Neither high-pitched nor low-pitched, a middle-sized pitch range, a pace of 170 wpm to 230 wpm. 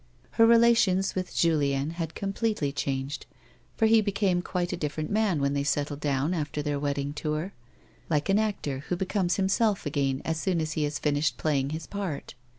Yes: medium, 160 Hz; average, 5.0 semitones; average, 180 wpm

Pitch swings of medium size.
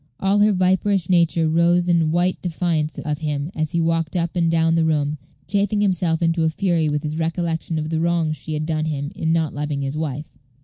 No: narrow, 2.0 semitones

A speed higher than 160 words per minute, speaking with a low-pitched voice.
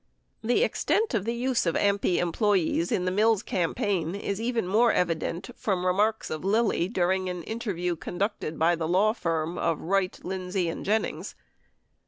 No: average, 170 wpm; high, 190 Hz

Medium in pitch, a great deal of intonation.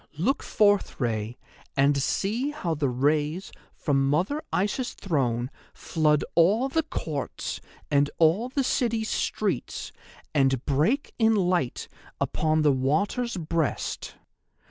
Yes: medium, 160 Hz; wide, 7.5 semitones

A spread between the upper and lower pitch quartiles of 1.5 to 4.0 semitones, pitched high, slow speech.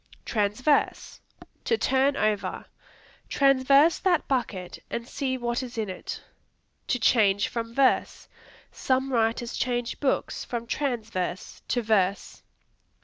Yes: average, 3.6 semitones; high, 240 Hz; slow, 115 wpm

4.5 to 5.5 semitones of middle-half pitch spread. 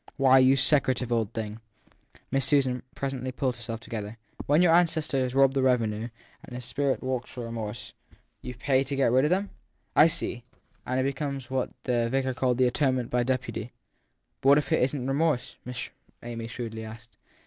No: narrow, 2.4 semitones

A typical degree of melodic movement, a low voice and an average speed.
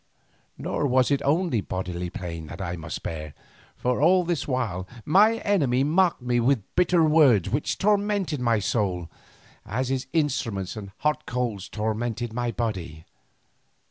No: wide, 7.7 semitones; low, 120 Hz; average, 145 wpm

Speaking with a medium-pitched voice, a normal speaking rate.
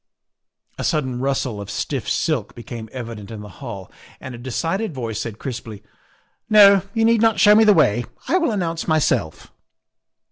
No: low, 130 Hz; average, 180 wpm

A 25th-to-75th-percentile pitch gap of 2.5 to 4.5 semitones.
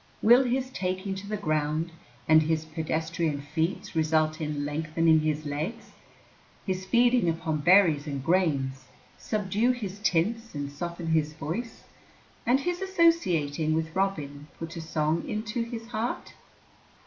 No: wide, 5.4 semitones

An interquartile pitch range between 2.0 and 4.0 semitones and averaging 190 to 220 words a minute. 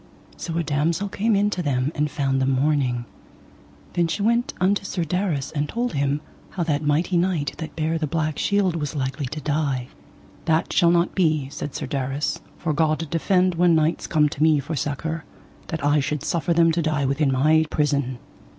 Yes: average, 3.0 semitones; average, 195 wpm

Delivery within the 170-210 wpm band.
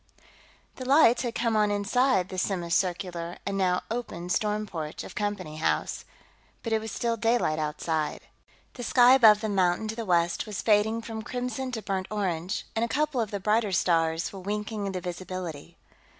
Yes: average, 180 wpm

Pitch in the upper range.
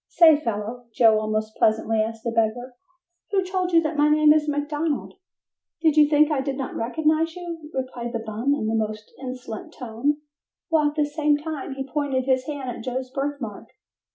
Yes: very high, 270 Hz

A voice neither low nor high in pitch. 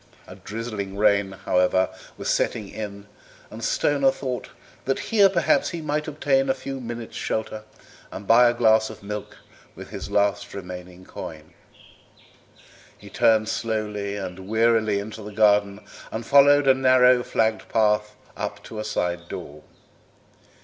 No: low, 110 Hz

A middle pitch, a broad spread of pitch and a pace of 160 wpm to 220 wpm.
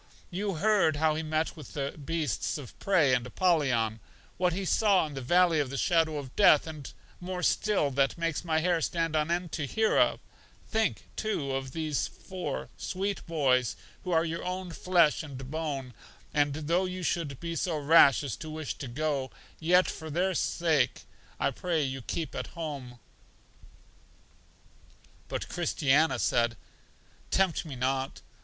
No: medium, 160 Hz; average, 4.1 semitones; average, 165 wpm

